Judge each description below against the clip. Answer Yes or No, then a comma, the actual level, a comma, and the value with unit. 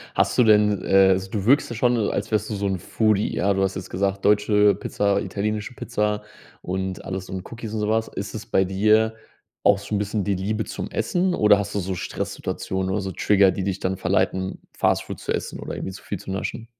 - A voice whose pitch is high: No, low, 100 Hz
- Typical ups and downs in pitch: No, narrow, 2.0 semitones